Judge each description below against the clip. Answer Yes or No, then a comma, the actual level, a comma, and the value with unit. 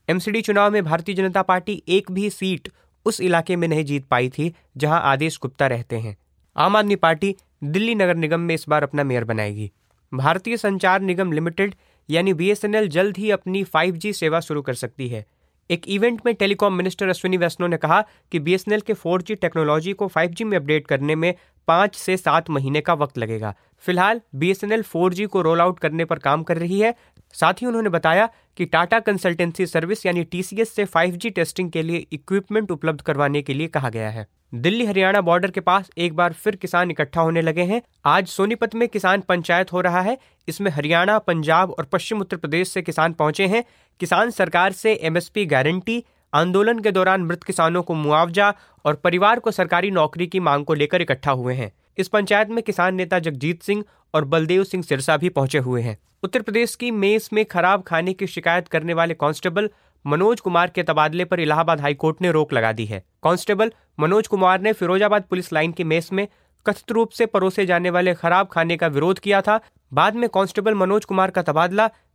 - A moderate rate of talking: No, fast, 195 wpm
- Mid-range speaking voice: Yes, medium, 180 Hz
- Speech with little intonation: No, average, 3.9 semitones